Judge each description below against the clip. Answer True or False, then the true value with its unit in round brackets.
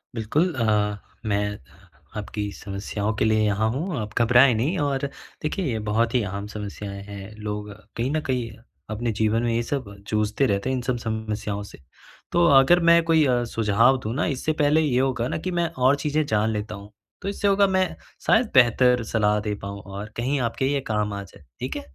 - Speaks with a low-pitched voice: True (115 Hz)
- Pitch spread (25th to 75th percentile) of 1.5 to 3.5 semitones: False (4.7 semitones)